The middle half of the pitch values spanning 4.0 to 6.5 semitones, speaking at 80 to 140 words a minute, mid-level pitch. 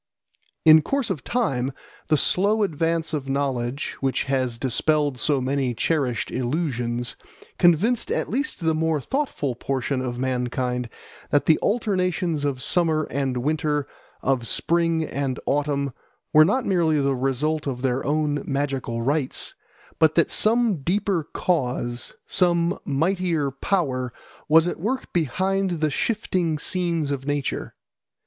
Yes: average, 4.4 semitones; slow, 135 wpm; medium, 150 Hz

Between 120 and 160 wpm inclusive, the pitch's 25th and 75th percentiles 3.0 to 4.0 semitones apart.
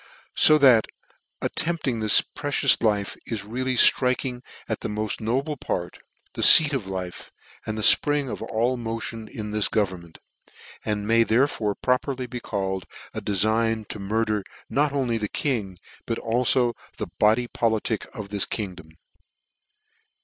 Yes: average, 145 wpm; average, 3.3 semitones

